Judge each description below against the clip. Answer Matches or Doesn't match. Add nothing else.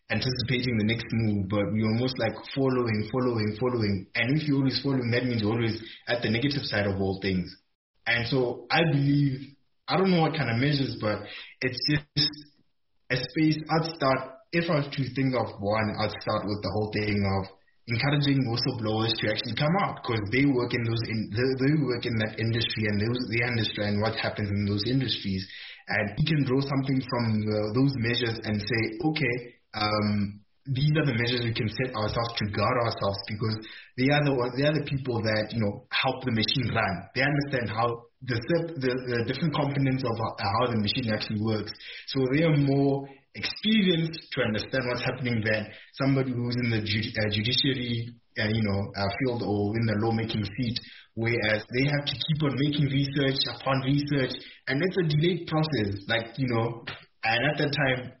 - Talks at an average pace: Matches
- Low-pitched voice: Matches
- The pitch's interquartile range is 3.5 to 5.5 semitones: Matches